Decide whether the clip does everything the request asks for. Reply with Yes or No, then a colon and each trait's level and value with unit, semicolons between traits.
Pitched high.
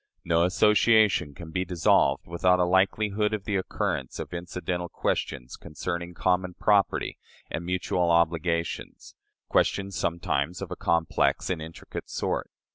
No: very low, 90 Hz